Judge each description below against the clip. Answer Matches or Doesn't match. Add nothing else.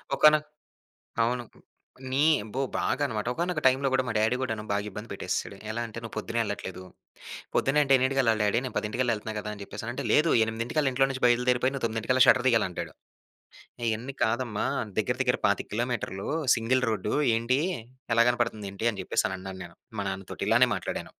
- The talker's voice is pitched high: Doesn't match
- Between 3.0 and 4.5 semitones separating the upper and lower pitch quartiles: Matches